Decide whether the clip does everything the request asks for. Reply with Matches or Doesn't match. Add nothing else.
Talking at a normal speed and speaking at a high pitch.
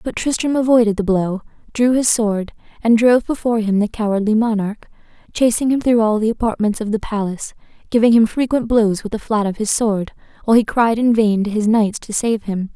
Doesn't match